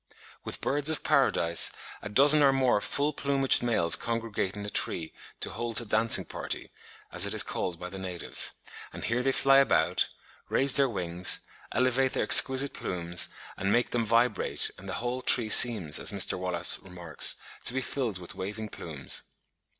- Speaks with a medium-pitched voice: No, low, 115 Hz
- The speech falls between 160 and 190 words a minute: Yes, average, 175 wpm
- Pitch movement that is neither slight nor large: No, wide, 6.1 semitones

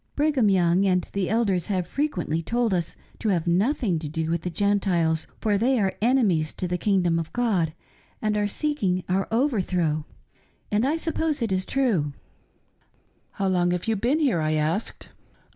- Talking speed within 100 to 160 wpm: No, average, 185 wpm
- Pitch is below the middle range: No, high, 195 Hz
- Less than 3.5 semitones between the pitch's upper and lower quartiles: No, average, 5.1 semitones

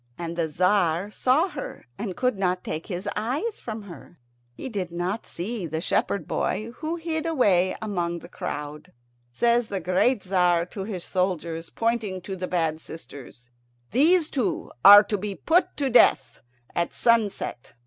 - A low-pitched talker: No, high, 190 Hz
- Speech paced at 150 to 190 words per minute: Yes, average, 160 wpm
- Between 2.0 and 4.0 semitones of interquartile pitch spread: No, average, 5.2 semitones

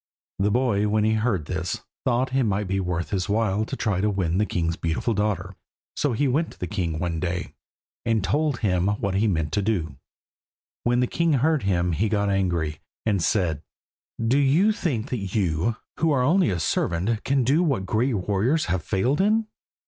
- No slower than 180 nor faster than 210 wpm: Yes, fast, 205 wpm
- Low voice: Yes, low, 105 Hz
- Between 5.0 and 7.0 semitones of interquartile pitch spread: Yes, wide, 5.5 semitones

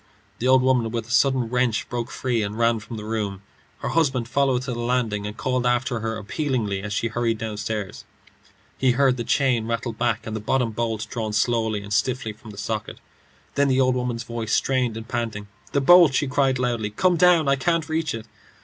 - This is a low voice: Yes, low, 120 Hz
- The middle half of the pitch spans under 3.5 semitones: Yes, average, 2.8 semitones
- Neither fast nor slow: No, fast, 210 wpm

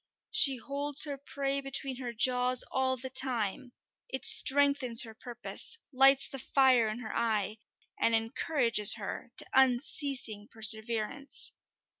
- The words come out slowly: Yes, slow, 130 wpm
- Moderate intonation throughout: Yes, average, 3.3 semitones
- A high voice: Yes, very high, 255 Hz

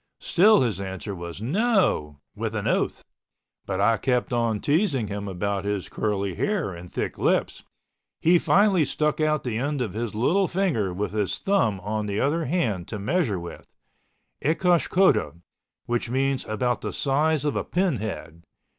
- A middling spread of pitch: No, wide, 7.8 semitones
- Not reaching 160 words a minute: No, average, 165 wpm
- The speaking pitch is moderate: No, low, 120 Hz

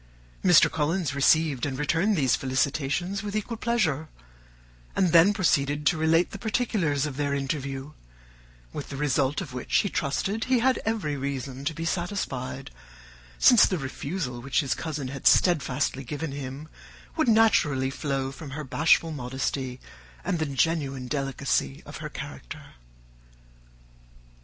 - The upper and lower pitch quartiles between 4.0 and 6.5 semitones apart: Yes, average, 4.4 semitones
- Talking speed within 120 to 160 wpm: Yes, average, 140 wpm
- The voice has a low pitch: No, medium, 145 Hz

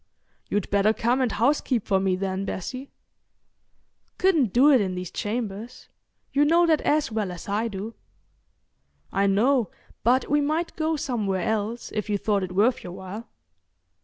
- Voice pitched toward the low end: No, high, 220 Hz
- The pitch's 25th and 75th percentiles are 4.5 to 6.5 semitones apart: Yes, average, 5.1 semitones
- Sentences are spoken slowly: No, average, 160 wpm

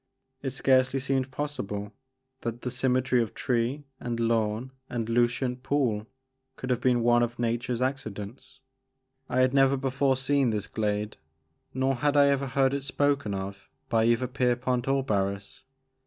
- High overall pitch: No, low, 125 Hz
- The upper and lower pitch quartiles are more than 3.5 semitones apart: No, narrow, 2.6 semitones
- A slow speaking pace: No, average, 155 wpm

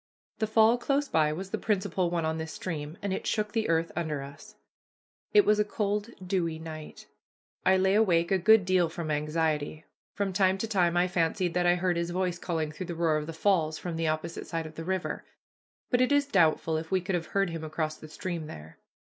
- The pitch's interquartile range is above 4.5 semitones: No, average, 3.3 semitones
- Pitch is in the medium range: Yes, medium, 175 Hz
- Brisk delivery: Yes, fast, 225 wpm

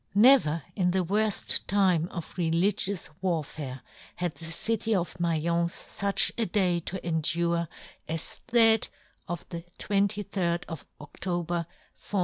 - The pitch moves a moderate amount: Yes, average, 3.1 semitones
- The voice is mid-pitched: Yes, medium, 175 Hz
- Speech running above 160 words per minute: No, slow, 135 wpm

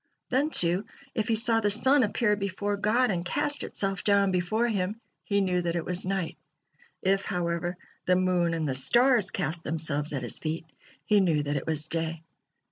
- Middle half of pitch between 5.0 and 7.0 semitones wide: No, average, 4.0 semitones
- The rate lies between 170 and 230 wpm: Yes, average, 190 wpm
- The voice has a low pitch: No, medium, 185 Hz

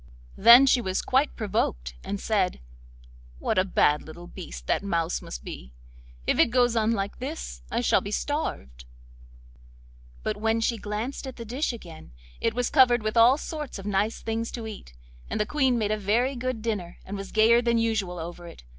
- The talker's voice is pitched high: Yes, high, 215 Hz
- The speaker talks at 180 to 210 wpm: Yes, average, 190 wpm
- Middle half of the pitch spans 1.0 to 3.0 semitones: No, average, 4.7 semitones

